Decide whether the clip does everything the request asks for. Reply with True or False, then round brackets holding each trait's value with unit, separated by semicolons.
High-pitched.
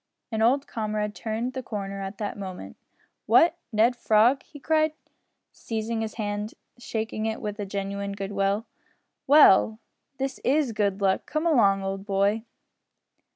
True (215 Hz)